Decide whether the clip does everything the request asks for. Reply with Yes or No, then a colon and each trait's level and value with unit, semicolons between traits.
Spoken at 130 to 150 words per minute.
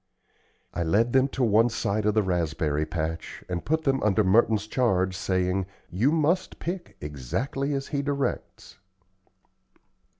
Yes: average, 140 wpm